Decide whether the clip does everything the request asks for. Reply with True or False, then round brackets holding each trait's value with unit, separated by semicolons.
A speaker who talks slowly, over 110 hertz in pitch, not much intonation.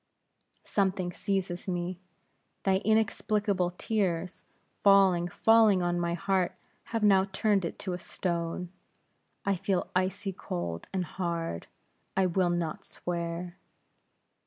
True (115 wpm; 185 Hz; 2.1 semitones)